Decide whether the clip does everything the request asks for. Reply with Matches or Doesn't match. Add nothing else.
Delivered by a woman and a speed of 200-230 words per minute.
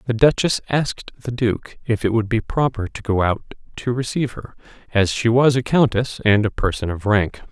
Doesn't match